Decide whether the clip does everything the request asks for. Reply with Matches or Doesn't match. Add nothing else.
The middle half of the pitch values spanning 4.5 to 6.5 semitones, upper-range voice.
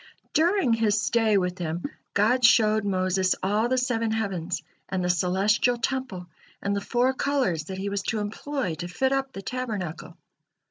Matches